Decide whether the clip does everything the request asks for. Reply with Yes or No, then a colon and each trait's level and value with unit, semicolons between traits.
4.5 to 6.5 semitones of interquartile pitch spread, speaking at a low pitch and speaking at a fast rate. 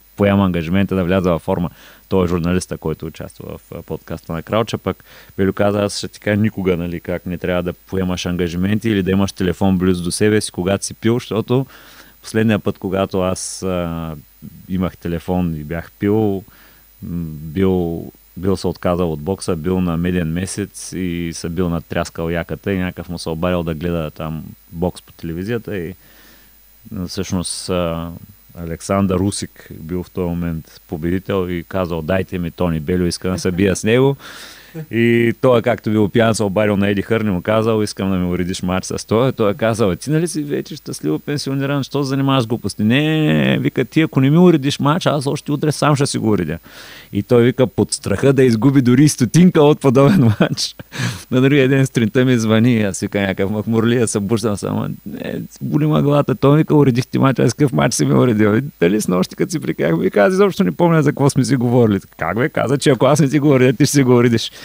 Yes: wide, 5.6 semitones; low, 100 Hz; fast, 205 wpm